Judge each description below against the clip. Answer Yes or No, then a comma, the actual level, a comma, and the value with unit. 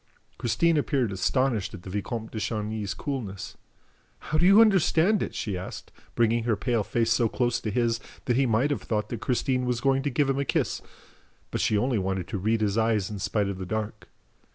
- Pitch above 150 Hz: No, low, 115 Hz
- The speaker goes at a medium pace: No, fast, 210 wpm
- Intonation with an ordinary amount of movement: Yes, average, 4.1 semitones